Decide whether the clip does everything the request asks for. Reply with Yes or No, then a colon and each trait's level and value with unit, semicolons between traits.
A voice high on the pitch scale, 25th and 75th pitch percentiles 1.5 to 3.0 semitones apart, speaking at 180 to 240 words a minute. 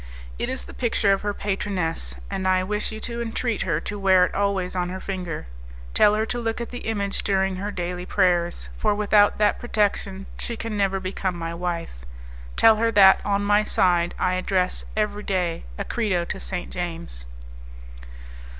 Yes: high, 195 Hz; narrow, 2.6 semitones; average, 185 wpm